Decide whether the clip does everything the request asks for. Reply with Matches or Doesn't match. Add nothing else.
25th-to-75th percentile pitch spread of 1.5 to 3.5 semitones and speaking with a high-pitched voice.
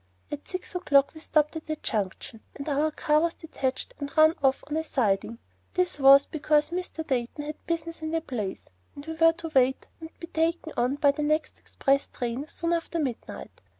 Matches